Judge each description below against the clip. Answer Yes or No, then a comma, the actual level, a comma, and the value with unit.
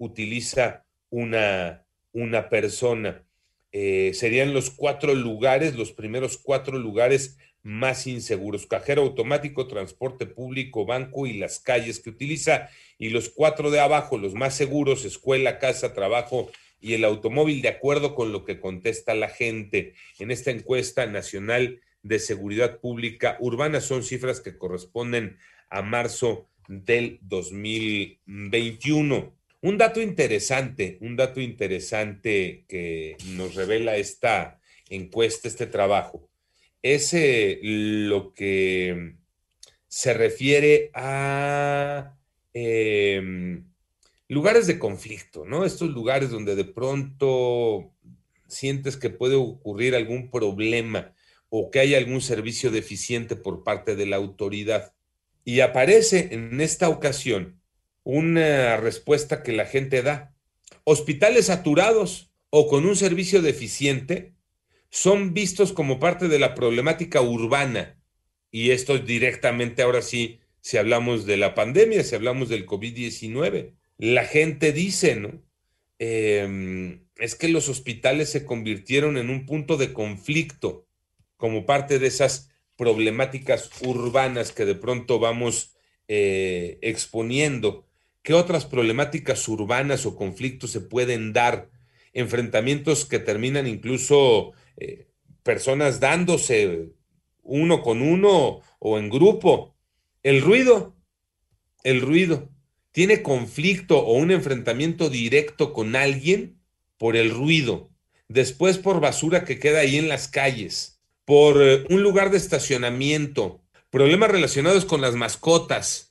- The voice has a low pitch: Yes, low, 125 Hz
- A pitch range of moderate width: Yes, average, 4.7 semitones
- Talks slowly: Yes, slow, 120 wpm